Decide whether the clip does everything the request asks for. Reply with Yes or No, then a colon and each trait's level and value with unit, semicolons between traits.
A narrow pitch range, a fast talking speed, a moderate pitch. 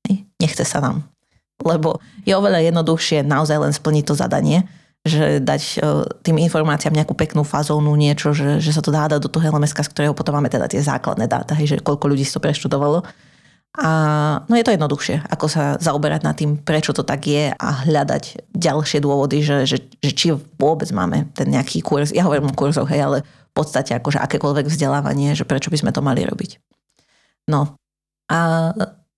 Yes: narrow, 1.9 semitones; fast, 185 wpm; medium, 150 Hz